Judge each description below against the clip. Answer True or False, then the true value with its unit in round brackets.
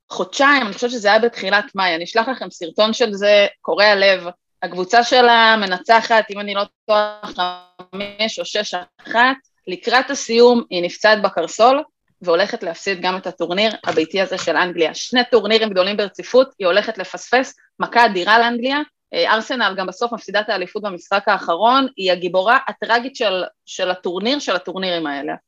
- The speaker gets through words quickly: True (160 wpm)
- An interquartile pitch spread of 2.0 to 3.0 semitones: False (4.4 semitones)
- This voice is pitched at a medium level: False (205 Hz)